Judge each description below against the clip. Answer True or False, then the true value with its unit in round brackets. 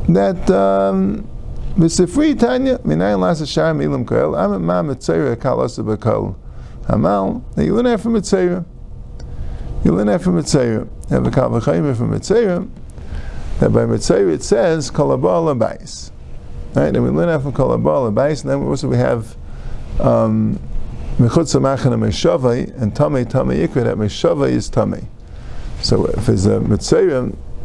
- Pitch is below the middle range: True (130 Hz)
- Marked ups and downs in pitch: True (8.0 semitones)